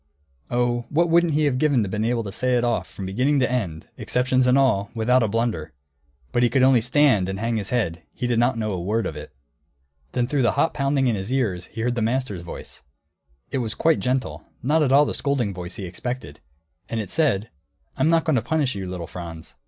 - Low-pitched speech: Yes, low, 120 Hz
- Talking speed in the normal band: No, fast, 230 wpm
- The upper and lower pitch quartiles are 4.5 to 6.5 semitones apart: Yes, average, 5.0 semitones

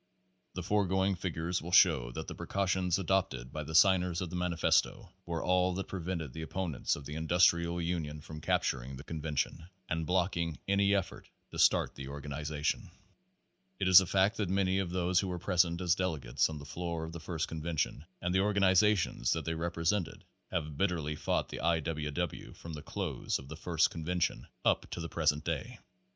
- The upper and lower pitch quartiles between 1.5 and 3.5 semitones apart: Yes, average, 2.9 semitones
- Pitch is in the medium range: No, very low, 85 Hz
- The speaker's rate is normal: Yes, average, 190 wpm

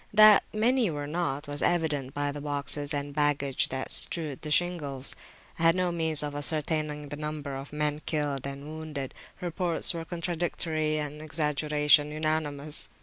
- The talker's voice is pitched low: No, medium, 150 Hz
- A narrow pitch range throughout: Yes, narrow, 2.0 semitones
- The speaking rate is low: No, average, 155 wpm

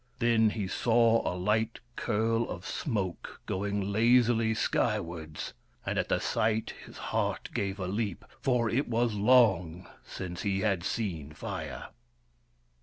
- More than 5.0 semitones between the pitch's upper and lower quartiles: No, average, 3.3 semitones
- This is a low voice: Yes, low, 110 Hz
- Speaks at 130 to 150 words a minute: Yes, slow, 135 wpm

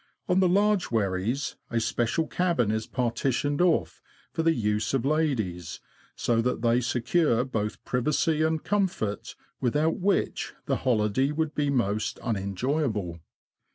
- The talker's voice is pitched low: Yes, low, 125 Hz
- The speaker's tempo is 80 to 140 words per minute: Yes, slow, 135 wpm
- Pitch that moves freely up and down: Yes, wide, 6.3 semitones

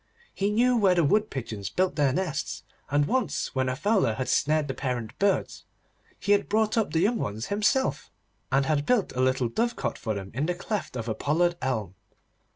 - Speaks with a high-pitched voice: No, medium, 155 Hz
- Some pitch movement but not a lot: No, wide, 8.1 semitones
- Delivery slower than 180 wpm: No, average, 200 wpm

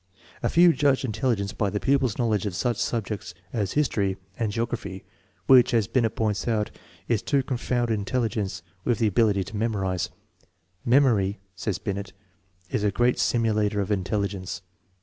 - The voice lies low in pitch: Yes, low, 110 Hz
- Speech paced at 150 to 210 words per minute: Yes, average, 165 wpm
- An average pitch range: Yes, average, 3.3 semitones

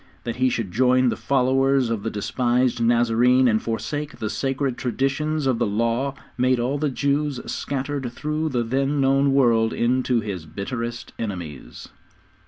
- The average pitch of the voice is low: Yes, low, 125 Hz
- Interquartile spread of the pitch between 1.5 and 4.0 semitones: Yes, average, 2.9 semitones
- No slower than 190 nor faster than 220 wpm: No, average, 155 wpm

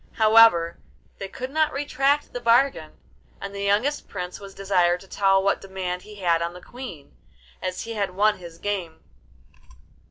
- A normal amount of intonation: Yes, average, 4.1 semitones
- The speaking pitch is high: Yes, high, 195 Hz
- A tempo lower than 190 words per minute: Yes, average, 165 wpm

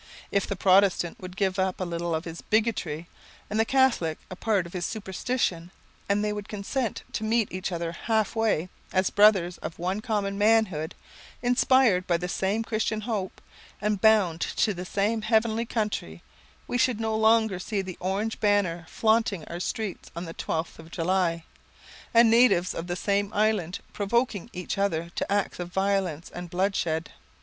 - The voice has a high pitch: Yes, high, 195 Hz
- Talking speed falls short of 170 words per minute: No, average, 175 wpm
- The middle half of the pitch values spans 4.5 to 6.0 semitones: No, average, 3.8 semitones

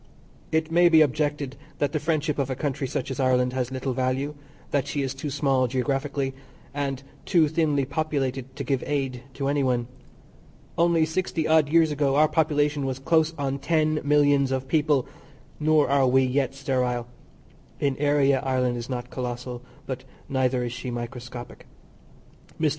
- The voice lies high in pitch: No, medium, 140 Hz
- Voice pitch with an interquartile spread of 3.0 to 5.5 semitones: No, narrow, 2.5 semitones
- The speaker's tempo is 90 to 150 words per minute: No, average, 165 wpm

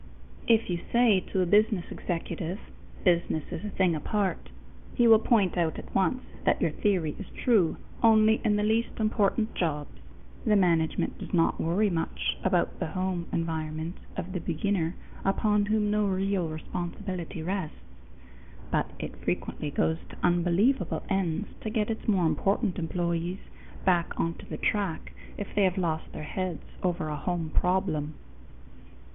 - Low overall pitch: No, medium, 185 Hz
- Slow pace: No, average, 155 wpm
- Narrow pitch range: No, average, 3.8 semitones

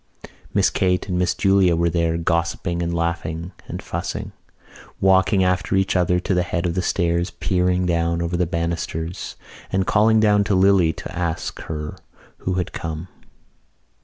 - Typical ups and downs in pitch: No, narrow, 1.9 semitones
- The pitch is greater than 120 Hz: No, very low, 90 Hz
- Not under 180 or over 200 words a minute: No, average, 160 wpm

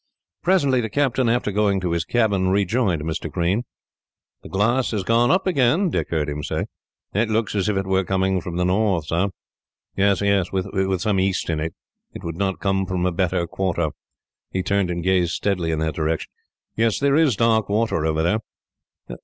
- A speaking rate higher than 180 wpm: Yes, average, 190 wpm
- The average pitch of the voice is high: No, very low, 95 Hz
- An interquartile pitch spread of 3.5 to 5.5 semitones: Yes, average, 4.1 semitones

